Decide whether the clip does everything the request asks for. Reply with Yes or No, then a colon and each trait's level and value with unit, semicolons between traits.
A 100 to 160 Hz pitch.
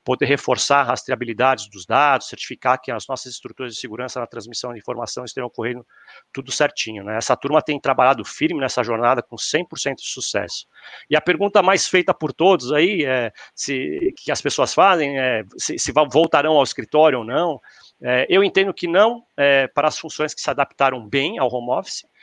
Yes: medium, 140 Hz